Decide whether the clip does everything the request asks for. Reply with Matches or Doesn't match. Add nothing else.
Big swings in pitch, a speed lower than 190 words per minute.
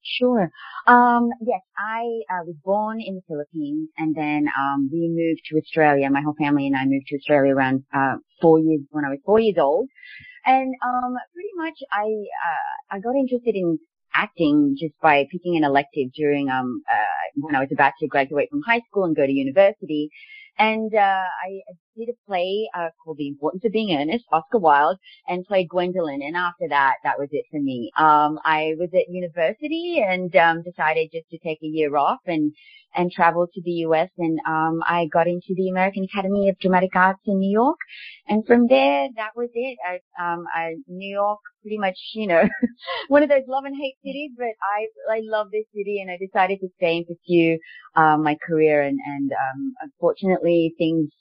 Doesn't match